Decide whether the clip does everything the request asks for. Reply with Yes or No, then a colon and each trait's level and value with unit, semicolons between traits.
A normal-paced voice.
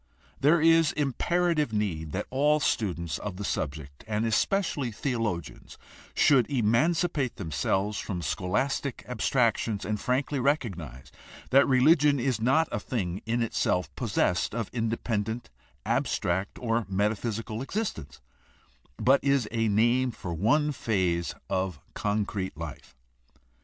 No: slow, 120 wpm